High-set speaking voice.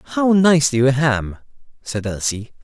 No: low, 135 Hz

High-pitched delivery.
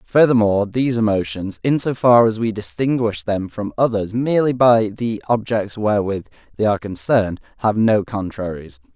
No: low, 110 Hz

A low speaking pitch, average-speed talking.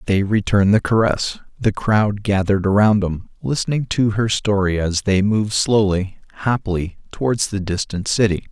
Yes: low, 100 Hz; average, 155 wpm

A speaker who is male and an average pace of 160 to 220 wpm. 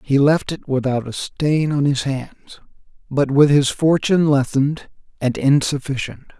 No: male; average, 150 wpm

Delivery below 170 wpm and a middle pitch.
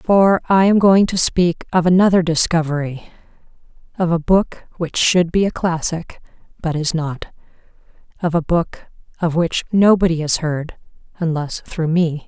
Yes: average, 150 wpm; medium, 170 Hz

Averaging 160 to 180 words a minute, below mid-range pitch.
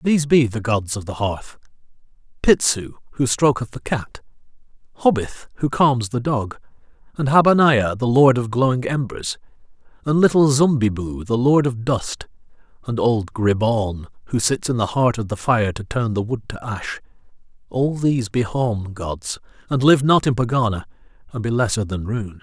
Yes: average, 165 wpm; low, 120 Hz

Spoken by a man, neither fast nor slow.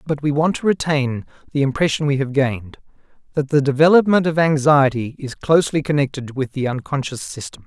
Yes: male; average, 170 wpm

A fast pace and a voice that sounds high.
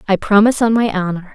Yes: fast, 225 wpm; high, 205 Hz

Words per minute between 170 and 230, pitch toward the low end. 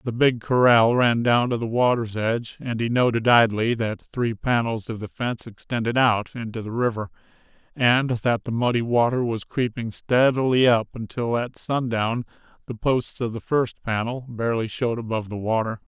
Yes: average, 175 wpm; low, 115 Hz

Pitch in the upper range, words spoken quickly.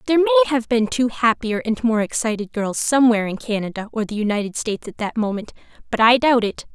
Yes: high, 230 Hz; fast, 215 wpm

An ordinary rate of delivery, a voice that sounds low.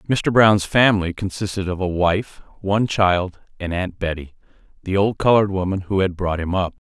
Yes: average, 185 wpm; very low, 95 Hz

